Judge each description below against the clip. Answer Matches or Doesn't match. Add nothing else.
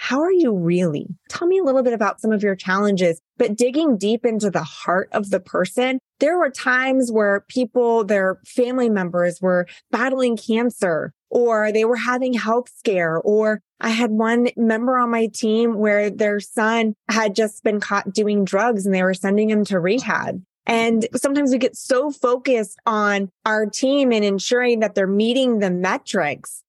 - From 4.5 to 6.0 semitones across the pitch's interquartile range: Doesn't match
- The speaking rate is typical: Matches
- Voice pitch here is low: Doesn't match